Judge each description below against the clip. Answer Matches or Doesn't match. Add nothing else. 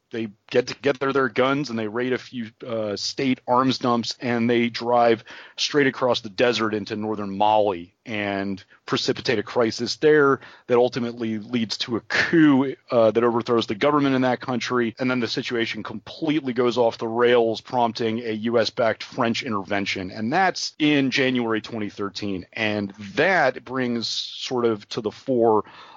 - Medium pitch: Doesn't match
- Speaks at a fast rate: Doesn't match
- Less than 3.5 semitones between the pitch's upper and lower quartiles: Matches